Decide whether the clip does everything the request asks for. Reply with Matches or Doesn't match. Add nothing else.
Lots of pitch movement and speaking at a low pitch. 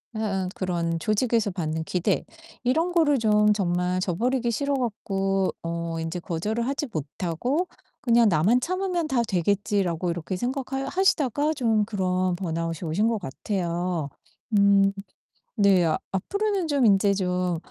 Doesn't match